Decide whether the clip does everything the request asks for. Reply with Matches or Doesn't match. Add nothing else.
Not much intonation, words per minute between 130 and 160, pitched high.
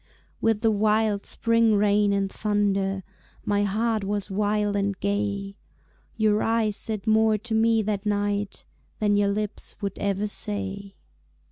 Matches